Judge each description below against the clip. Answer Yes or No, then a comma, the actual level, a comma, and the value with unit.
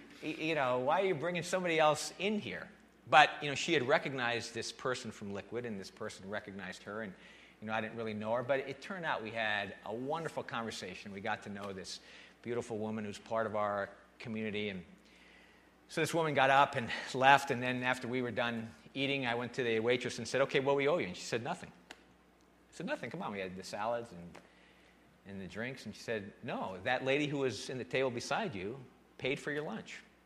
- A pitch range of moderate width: Yes, average, 4.7 semitones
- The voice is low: Yes, low, 115 Hz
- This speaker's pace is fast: Yes, fast, 230 wpm